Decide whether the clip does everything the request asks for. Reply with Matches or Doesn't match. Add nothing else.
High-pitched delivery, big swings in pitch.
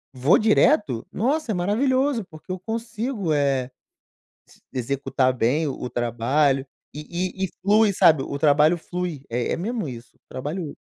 Doesn't match